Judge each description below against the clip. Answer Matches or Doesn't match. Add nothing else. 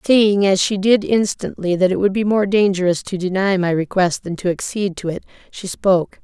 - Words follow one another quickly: Matches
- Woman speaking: Matches